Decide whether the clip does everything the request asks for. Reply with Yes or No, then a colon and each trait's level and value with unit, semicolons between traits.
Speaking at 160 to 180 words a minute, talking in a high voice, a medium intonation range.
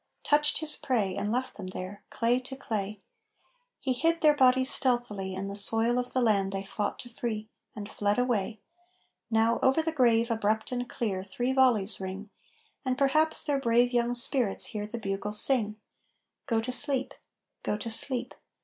Yes: average, 175 wpm; high, 235 Hz; average, 3.7 semitones